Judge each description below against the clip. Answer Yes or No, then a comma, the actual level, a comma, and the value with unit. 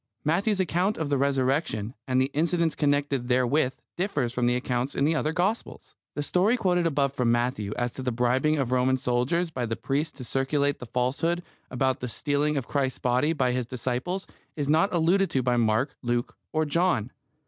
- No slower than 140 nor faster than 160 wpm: No, average, 190 wpm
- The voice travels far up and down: No, average, 4.3 semitones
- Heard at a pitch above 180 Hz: No, medium, 140 Hz